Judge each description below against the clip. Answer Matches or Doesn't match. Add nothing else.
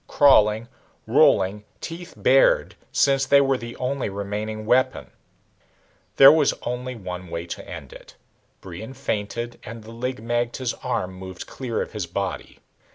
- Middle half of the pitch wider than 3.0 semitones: Matches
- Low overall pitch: Matches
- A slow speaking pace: Doesn't match